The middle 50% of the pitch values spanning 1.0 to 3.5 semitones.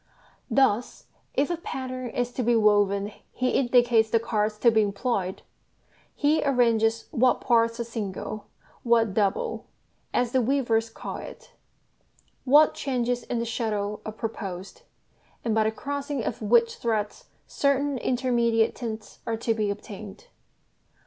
Yes: average, 2.7 semitones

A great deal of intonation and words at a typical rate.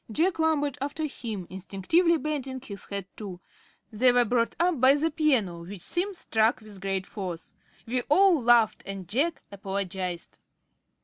Yes: wide, 7.3 semitones; average, 150 wpm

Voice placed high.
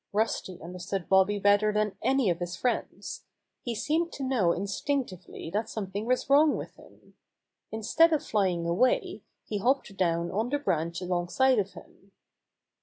Yes: high, 205 Hz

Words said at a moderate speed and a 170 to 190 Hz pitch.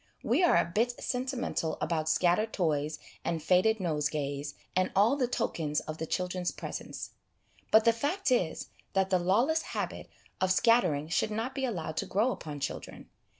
Yes: average, 165 wpm; medium, 185 Hz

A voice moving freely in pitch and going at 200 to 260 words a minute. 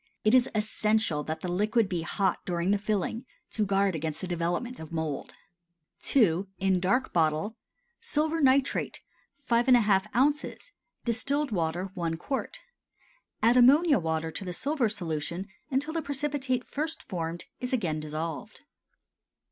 No: wide, 7.1 semitones; average, 140 wpm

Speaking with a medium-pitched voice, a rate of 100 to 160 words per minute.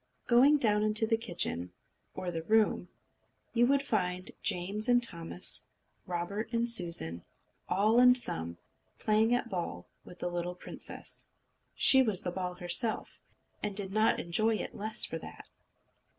No: high, 205 Hz; average, 155 wpm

